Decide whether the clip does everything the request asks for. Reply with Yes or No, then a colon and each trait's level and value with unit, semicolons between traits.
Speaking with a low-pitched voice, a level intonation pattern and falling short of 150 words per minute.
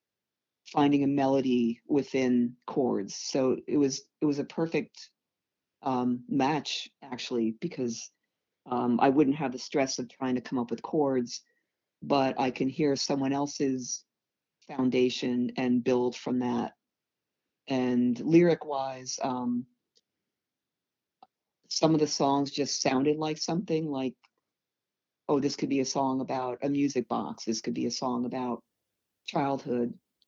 Yes: low, 130 Hz; narrow, 2.3 semitones; average, 140 wpm